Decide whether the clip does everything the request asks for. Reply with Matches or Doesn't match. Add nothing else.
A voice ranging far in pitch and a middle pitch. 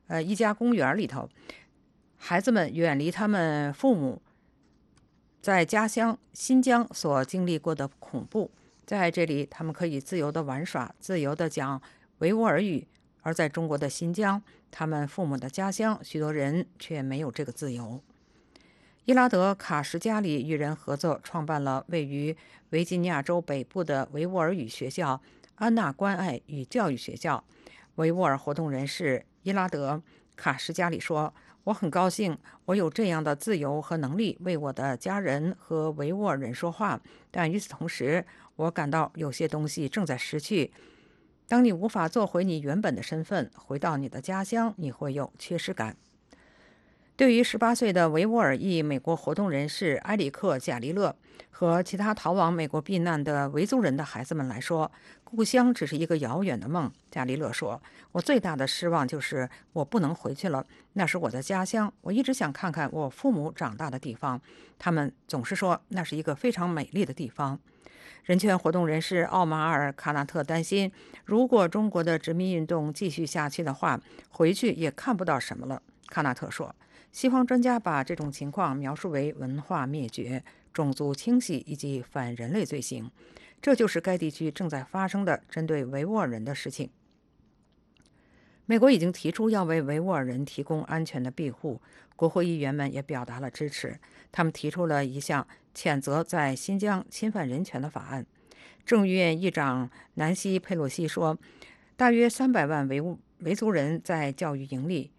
Doesn't match